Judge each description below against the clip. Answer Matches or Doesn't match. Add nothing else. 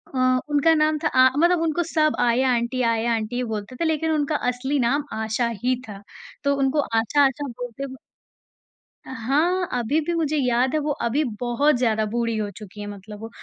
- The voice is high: Matches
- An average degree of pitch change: Matches